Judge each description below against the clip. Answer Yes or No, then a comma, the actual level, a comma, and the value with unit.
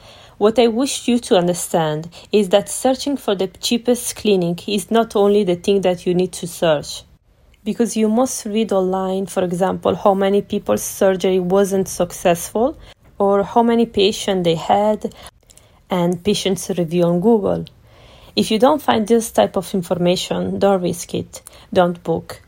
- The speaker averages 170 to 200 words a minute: No, average, 160 wpm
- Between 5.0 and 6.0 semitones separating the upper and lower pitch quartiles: No, average, 3.5 semitones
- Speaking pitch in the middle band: No, high, 195 Hz